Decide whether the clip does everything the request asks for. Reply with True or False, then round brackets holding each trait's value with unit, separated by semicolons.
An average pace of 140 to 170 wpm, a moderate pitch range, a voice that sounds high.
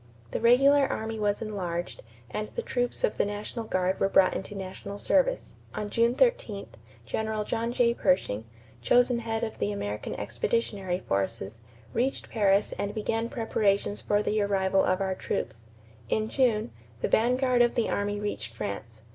True (160 wpm; 3.6 semitones; 210 Hz)